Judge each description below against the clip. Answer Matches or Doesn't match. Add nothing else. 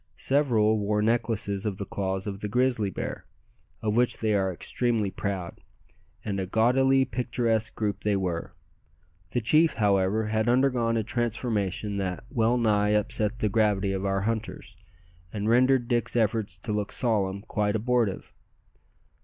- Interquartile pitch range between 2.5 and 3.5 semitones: Matches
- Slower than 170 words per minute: Matches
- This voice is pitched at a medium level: Doesn't match